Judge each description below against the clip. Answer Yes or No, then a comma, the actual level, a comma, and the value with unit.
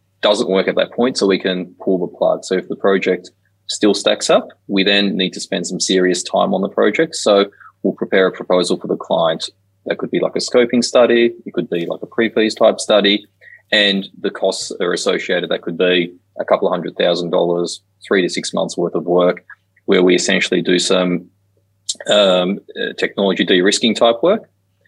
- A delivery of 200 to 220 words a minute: Yes, fast, 205 wpm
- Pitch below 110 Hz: Yes, very low, 95 Hz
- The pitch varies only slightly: Yes, narrow, 2.1 semitones